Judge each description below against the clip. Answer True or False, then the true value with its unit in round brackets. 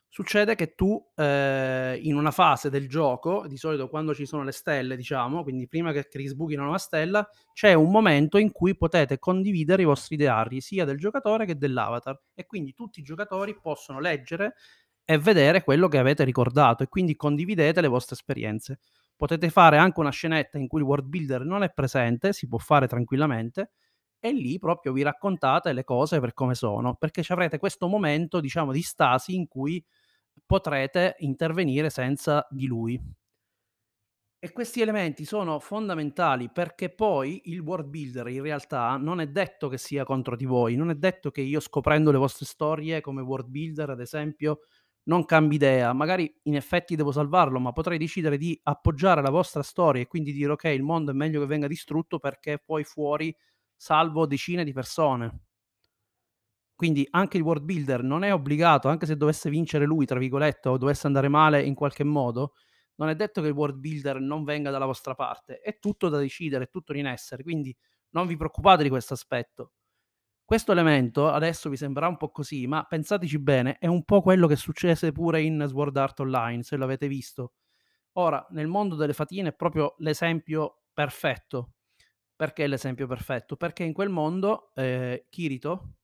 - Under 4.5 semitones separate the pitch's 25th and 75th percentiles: True (3.8 semitones)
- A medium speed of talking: False (180 wpm)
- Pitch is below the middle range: False (150 Hz)